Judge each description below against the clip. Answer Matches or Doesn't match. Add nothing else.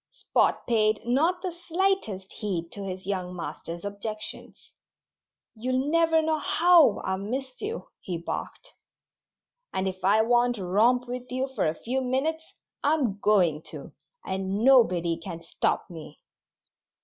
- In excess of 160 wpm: Doesn't match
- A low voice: Doesn't match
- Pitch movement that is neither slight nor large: Doesn't match